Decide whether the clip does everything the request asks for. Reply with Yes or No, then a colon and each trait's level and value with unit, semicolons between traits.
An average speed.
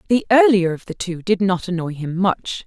No: fast, 225 wpm